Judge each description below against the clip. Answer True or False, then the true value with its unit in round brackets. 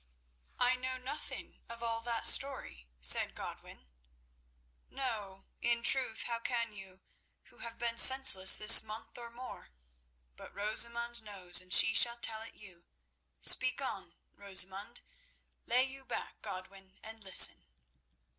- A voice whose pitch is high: True (230 Hz)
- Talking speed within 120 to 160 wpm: True (135 wpm)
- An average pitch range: True (3.4 semitones)